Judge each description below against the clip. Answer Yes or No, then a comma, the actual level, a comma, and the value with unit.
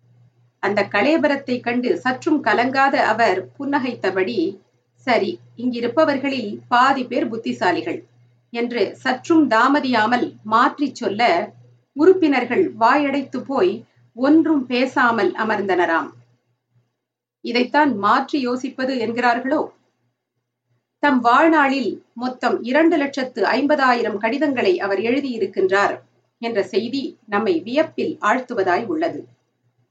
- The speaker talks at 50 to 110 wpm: Yes, average, 85 wpm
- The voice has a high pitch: Yes, high, 245 Hz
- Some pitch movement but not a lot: No, wide, 7.2 semitones